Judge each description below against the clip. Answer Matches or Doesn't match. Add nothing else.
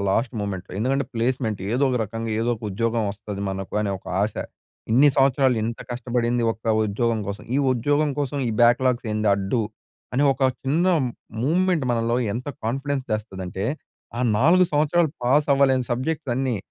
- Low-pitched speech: Matches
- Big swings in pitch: Doesn't match